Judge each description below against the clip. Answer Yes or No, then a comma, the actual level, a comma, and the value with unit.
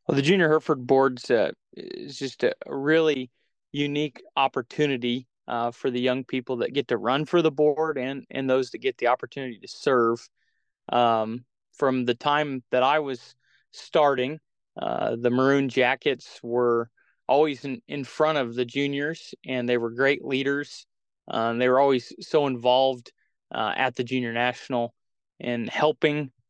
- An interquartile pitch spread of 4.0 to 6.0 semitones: No, average, 2.8 semitones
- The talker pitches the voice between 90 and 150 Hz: Yes, low, 130 Hz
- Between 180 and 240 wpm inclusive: No, average, 160 wpm